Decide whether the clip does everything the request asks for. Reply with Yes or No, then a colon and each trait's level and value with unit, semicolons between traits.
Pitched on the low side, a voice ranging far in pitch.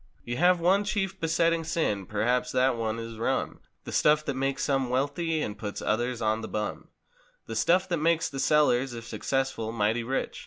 Yes: low, 130 Hz; wide, 5.9 semitones